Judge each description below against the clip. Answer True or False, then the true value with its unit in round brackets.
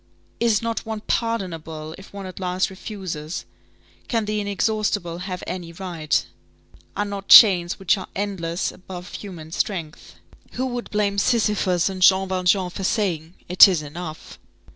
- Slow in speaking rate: False (145 wpm)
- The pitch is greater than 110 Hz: True (190 Hz)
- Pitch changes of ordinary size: True (3.0 semitones)